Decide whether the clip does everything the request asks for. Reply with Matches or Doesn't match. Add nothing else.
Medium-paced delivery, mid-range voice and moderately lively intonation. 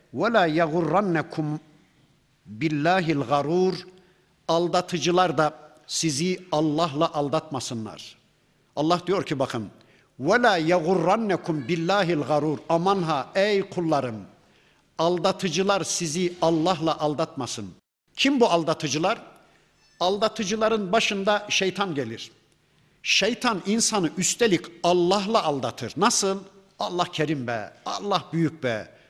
Doesn't match